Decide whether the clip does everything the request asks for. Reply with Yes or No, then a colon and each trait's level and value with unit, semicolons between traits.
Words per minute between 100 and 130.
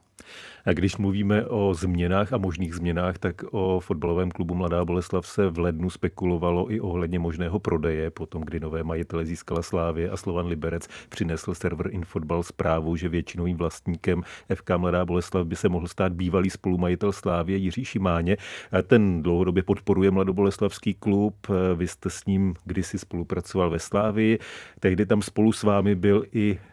No: average, 155 wpm